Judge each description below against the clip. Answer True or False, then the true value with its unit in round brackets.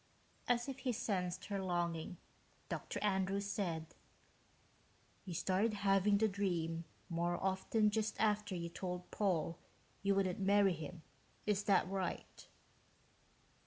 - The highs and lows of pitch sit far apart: False (2.7 semitones)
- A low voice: False (190 Hz)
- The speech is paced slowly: True (125 wpm)